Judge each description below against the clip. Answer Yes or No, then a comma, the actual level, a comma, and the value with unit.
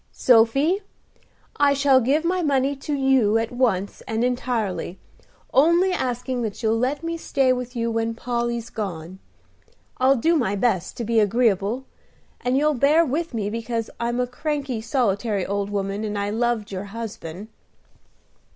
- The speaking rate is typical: Yes, average, 155 wpm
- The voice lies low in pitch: No, high, 240 Hz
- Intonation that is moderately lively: Yes, average, 3.9 semitones